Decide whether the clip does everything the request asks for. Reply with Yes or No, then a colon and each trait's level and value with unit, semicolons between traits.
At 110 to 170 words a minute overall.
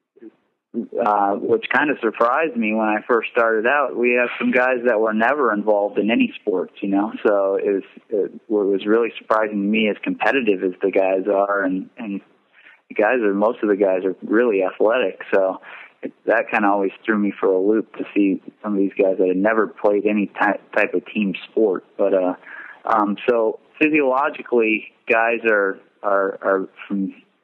No: average, 190 wpm